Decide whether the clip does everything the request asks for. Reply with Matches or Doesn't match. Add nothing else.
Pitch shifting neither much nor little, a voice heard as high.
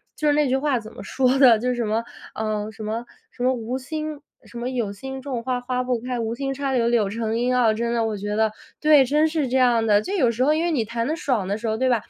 Matches